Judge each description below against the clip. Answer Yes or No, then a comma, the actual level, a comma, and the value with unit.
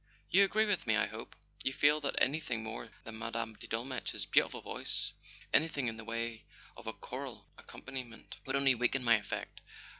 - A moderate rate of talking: Yes, average, 185 wpm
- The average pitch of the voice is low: Yes, low, 120 Hz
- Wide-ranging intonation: No, average, 3.4 semitones